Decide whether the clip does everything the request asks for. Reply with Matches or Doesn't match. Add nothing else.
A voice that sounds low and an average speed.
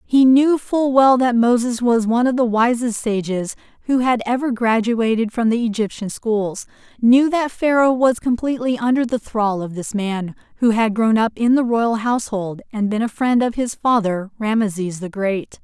Doesn't match